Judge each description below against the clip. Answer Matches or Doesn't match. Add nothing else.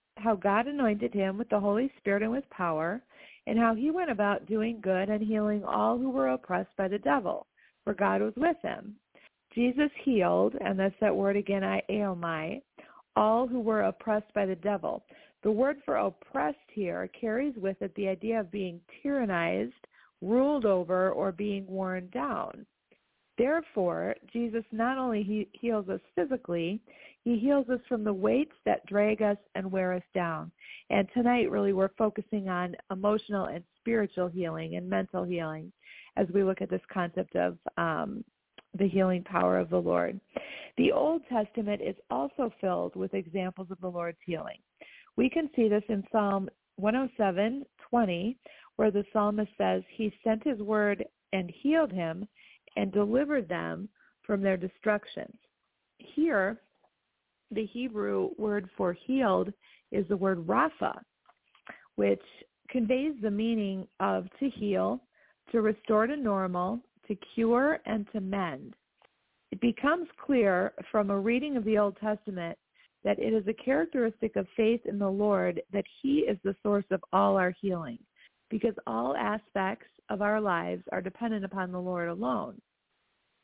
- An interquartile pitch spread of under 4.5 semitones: Matches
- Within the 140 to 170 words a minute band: Matches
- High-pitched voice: Matches